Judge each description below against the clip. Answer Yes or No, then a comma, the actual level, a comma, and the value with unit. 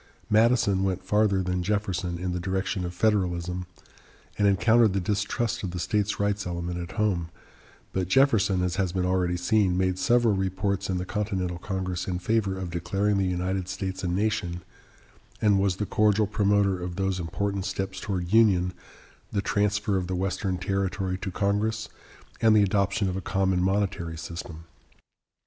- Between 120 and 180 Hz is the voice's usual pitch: No, very low, 95 Hz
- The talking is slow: No, average, 165 wpm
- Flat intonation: Yes, narrow, 2.2 semitones